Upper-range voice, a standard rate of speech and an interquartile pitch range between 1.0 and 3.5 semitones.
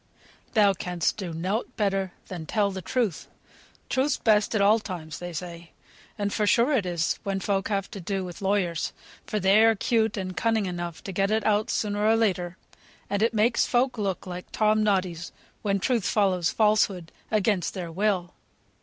Yes: high, 200 Hz; average, 180 wpm; average, 3.1 semitones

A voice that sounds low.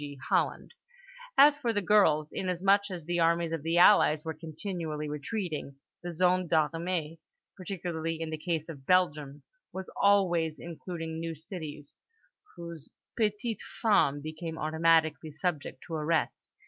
No: medium, 165 Hz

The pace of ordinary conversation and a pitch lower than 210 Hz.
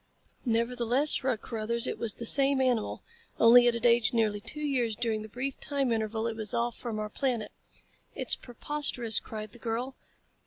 No: average, 180 wpm; high, 235 Hz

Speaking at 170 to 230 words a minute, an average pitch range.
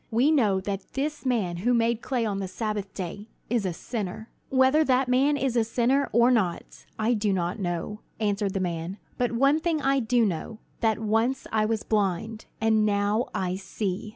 Yes: average, 190 wpm; average, 4.0 semitones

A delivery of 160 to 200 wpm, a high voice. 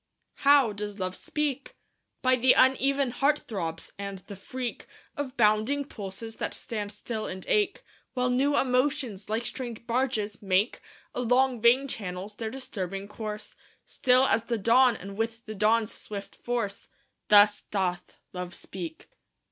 No: average, 145 wpm; high, 225 Hz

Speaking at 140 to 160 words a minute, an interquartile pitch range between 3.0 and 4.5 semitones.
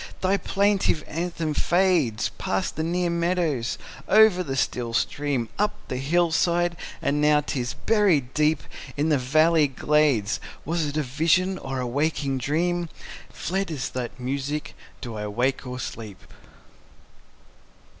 No: average, 145 wpm; average, 5.0 semitones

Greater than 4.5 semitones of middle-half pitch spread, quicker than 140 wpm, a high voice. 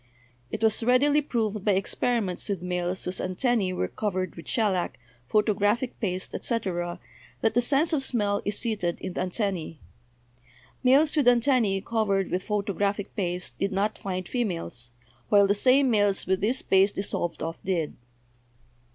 No: average, 4.0 semitones; average, 150 wpm; high, 200 Hz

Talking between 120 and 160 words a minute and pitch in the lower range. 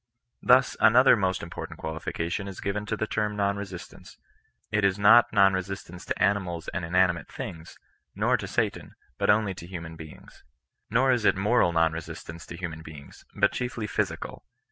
No: average, 175 wpm; very low, 95 Hz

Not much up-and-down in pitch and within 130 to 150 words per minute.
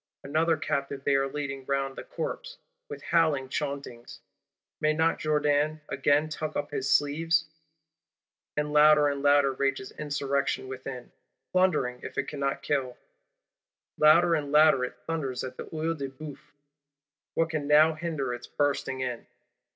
Yes: narrow, 2.2 semitones; average, 145 wpm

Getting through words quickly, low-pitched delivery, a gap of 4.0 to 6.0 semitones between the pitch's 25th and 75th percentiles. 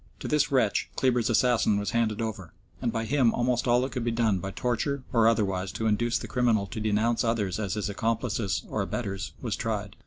No: fast, 210 wpm; low, 115 Hz; average, 2.9 semitones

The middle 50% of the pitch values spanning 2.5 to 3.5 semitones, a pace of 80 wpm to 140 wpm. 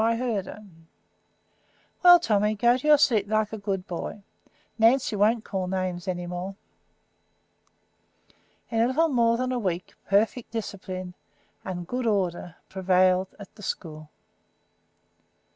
No: average, 3.9 semitones; slow, 135 wpm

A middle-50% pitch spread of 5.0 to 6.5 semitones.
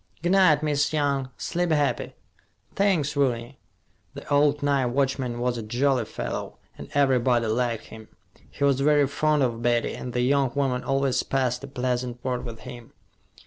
No: average, 2.7 semitones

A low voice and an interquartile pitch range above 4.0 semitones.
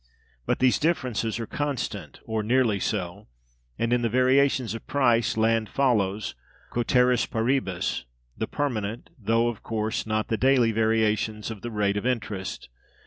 No: low, 115 Hz; average, 2.7 semitones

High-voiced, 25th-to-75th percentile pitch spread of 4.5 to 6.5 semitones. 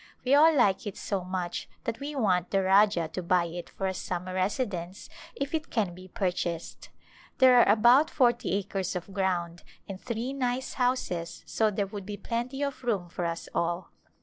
Yes: high, 195 Hz; average, 5.3 semitones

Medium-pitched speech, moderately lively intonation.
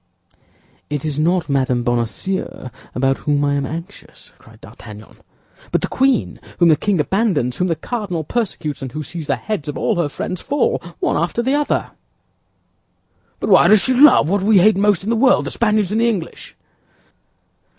No: medium, 175 Hz; wide, 6.8 semitones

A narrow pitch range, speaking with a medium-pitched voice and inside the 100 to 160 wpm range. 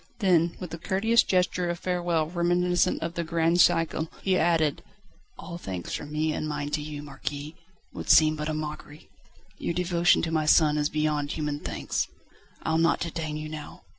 No: narrow, 2.2 semitones; medium, 160 Hz; average, 180 wpm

